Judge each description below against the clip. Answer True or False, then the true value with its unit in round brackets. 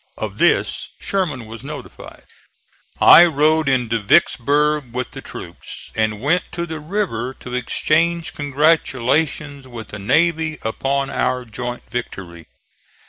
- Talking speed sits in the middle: False (125 wpm)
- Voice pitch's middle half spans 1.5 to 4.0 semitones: False (4.6 semitones)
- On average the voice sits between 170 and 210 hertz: False (140 Hz)